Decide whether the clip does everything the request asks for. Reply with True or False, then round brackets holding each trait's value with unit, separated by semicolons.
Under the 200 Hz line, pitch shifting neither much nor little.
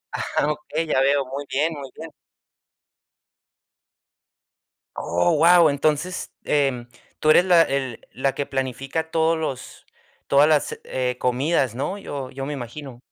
True (140 Hz; 3.2 semitones)